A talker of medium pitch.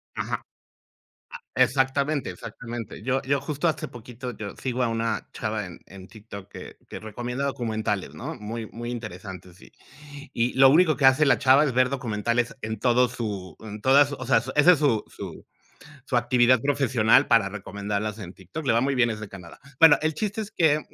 No: low, 120 Hz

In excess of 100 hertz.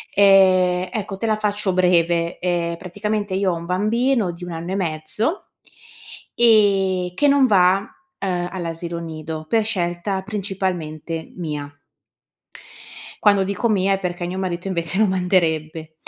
Yes: medium, 185 Hz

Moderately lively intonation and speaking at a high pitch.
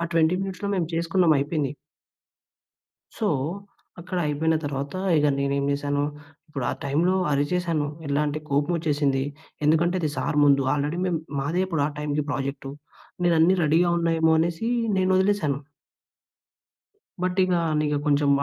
No: average, 3.3 semitones; medium, 155 Hz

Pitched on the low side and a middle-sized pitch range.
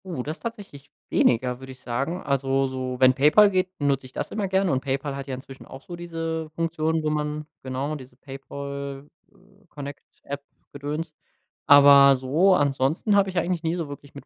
No: medium, 145 Hz; average, 3.5 semitones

